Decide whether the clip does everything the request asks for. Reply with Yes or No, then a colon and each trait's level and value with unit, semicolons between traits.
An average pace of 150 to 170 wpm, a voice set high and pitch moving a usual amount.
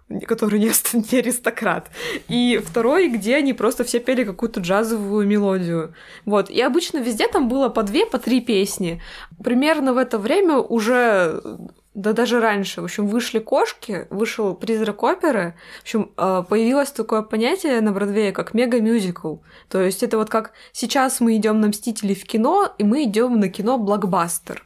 Yes: fast, 160 wpm; high, 225 Hz; average, 3.3 semitones